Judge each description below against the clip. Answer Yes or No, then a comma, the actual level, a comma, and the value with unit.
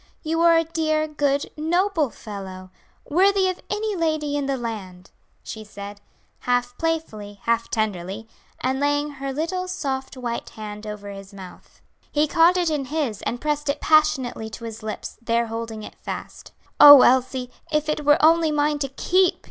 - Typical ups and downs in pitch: No, wide, 5.9 semitones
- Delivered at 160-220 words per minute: Yes, average, 170 wpm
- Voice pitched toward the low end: No, very high, 275 Hz